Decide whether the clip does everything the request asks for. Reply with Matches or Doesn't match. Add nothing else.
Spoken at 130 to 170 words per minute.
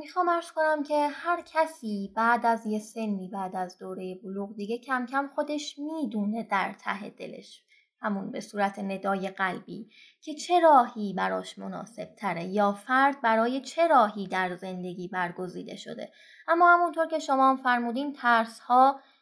Matches